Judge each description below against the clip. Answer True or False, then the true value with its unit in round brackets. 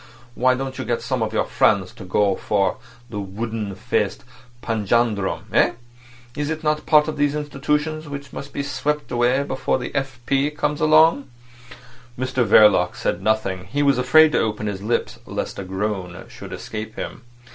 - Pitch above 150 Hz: False (125 Hz)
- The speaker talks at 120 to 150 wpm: False (170 wpm)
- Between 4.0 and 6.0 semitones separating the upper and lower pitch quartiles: True (5.6 semitones)